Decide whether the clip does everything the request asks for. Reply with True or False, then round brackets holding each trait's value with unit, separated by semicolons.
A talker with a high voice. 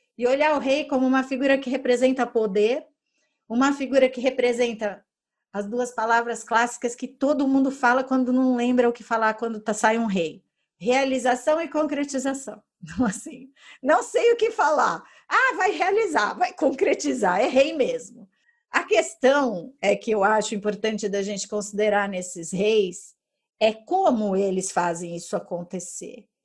True (245 Hz)